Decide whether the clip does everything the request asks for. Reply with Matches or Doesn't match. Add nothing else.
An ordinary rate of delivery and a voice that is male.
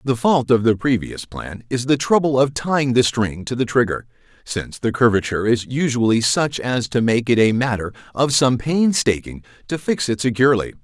Matches